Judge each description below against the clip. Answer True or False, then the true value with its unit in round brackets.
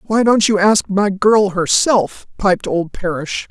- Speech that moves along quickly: False (170 wpm)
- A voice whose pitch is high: True (195 Hz)